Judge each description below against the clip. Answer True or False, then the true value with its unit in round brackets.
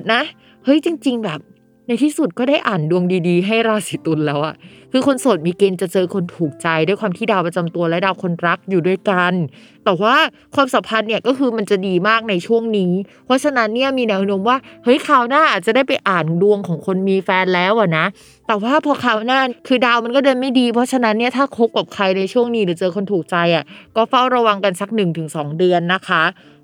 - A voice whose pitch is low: False (205 Hz)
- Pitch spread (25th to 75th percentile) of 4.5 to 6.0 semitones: True (5.4 semitones)